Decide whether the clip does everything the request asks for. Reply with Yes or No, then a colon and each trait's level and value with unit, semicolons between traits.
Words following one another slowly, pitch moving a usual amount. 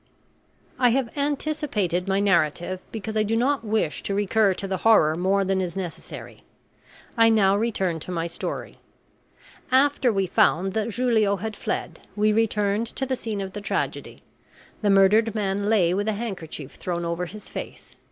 No: average, 170 wpm; average, 3.1 semitones